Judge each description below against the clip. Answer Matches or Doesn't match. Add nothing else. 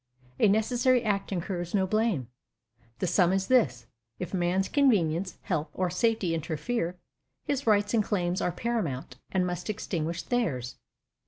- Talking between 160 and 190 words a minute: Doesn't match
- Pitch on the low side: Doesn't match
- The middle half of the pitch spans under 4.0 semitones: Doesn't match